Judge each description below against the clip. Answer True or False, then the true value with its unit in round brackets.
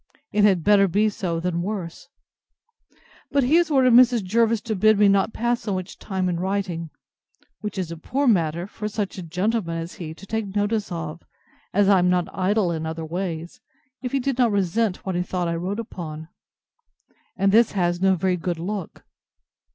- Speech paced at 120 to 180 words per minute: False (190 wpm)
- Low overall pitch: False (190 Hz)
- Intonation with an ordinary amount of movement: True (3.9 semitones)